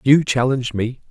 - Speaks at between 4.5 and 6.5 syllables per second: Yes, 5.3 syllables/s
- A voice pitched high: No, low, 125 Hz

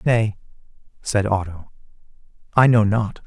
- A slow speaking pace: Yes, slow, 110 wpm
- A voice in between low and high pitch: No, low, 105 Hz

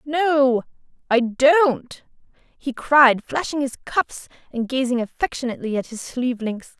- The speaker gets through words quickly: No, slow, 135 wpm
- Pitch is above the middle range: Yes, very high, 260 Hz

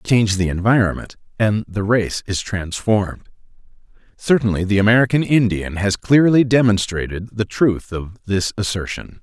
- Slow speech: Yes, slow, 130 wpm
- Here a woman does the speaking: No, male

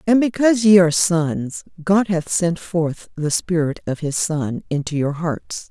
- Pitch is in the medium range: Yes, medium, 170 Hz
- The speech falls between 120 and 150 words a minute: No, average, 180 wpm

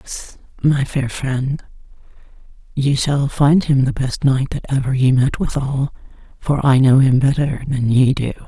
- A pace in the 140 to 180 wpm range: Yes, average, 170 wpm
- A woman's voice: Yes, female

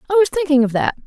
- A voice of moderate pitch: No, very high, 295 Hz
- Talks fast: Yes, fast, 280 wpm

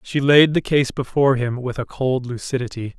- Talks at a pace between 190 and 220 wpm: Yes, average, 200 wpm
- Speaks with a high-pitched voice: No, low, 130 Hz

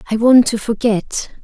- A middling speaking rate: Yes, average, 165 wpm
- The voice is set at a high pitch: Yes, high, 225 Hz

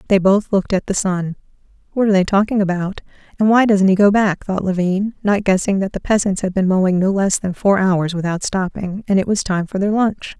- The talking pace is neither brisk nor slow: No, fast, 235 wpm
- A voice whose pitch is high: Yes, high, 195 Hz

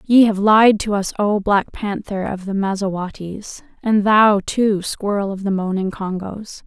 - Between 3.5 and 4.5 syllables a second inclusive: Yes, 4.2 syllables/s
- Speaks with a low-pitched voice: No, high, 200 Hz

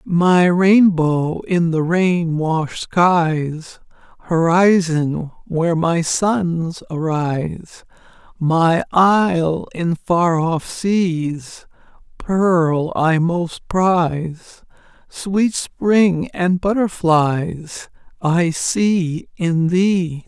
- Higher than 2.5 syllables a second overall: No, 2.4 syllables/s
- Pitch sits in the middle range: Yes, medium, 170 Hz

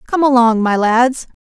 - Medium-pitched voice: No, high, 245 Hz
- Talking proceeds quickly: No, average, 170 wpm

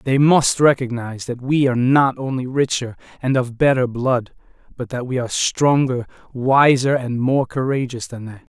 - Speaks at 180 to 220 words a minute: No, average, 170 wpm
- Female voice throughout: No, male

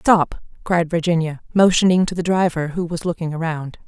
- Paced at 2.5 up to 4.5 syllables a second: No, 5.3 syllables/s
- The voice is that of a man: No, female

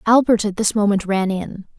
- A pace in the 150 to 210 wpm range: Yes, average, 200 wpm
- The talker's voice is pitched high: Yes, high, 210 Hz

